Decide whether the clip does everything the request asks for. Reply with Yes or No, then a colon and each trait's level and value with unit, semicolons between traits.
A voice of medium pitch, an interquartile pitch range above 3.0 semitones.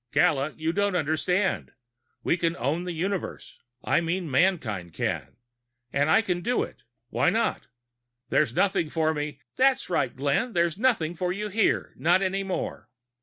Yes: medium, 170 Hz; average, 3.9 semitones